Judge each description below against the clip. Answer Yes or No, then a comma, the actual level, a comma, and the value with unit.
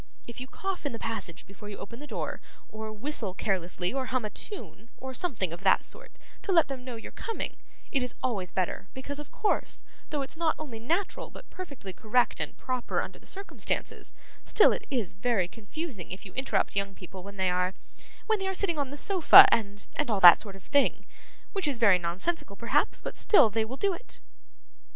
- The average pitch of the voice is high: Yes, high, 235 Hz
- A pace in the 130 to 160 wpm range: No, fast, 205 wpm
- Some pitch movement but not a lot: No, wide, 7.0 semitones